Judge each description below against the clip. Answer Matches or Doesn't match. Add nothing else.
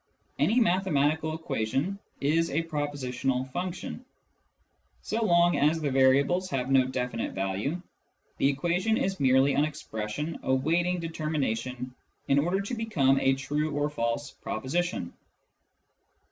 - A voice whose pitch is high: Doesn't match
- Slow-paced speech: Matches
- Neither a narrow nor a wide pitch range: Matches